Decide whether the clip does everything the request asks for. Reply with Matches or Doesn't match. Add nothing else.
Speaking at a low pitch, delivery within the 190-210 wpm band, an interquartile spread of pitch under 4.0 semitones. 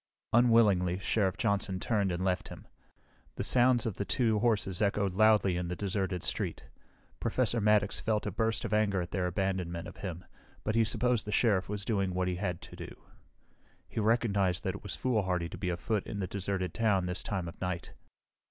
Matches